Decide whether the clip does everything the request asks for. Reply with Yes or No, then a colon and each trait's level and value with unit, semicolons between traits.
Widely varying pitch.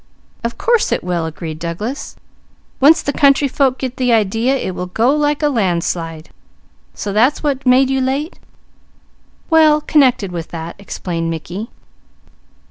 Yes: wide, 7.8 semitones